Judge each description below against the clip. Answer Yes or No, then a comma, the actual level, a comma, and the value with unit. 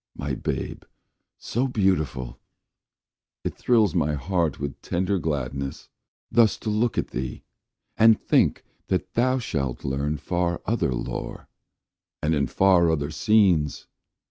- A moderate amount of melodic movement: No, wide, 6.9 semitones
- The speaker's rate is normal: No, slow, 125 wpm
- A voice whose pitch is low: Yes, very low, 85 Hz